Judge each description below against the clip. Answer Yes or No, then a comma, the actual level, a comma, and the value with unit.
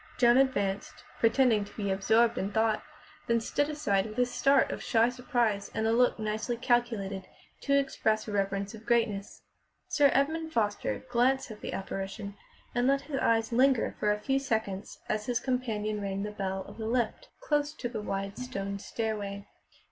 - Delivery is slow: No, average, 175 wpm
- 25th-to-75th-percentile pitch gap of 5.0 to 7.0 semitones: No, average, 3.7 semitones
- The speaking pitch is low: No, high, 225 Hz